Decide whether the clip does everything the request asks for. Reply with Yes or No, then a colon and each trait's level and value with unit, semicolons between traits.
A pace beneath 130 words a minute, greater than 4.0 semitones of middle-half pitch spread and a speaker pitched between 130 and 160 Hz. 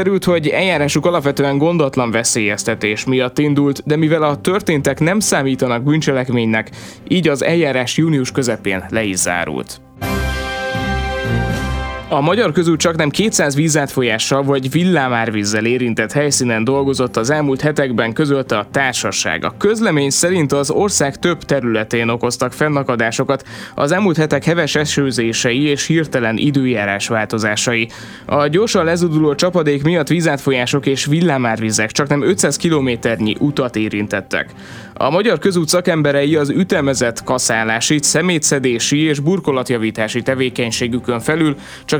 Yes: average, 120 wpm; average, 5.1 semitones; medium, 140 Hz